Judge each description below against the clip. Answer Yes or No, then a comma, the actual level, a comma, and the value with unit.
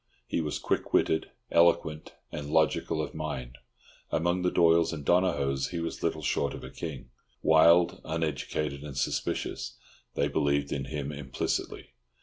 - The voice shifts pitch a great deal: No, average, 2.7 semitones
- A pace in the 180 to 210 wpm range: No, average, 145 wpm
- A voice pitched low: Yes, very low, 80 Hz